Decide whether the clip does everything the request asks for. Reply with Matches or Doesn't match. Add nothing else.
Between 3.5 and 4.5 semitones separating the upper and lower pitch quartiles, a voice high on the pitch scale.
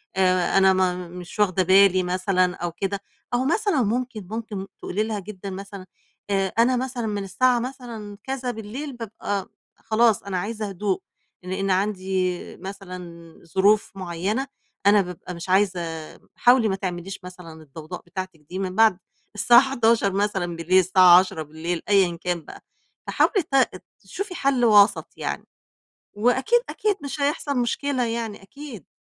Matches